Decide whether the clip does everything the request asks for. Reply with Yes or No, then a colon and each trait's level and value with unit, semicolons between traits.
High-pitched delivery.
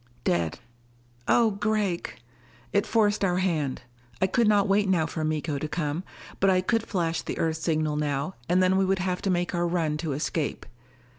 No: medium, 175 Hz